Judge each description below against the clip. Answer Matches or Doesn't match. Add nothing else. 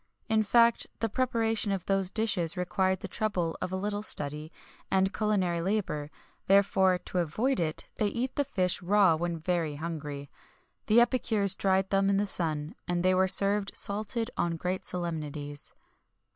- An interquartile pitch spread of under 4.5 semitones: Matches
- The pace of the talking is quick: Doesn't match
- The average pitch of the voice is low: Doesn't match